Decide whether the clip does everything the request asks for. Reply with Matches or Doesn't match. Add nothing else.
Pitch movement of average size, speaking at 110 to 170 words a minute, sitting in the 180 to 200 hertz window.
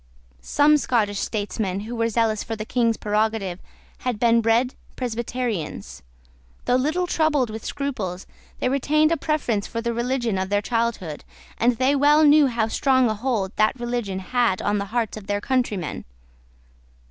Doesn't match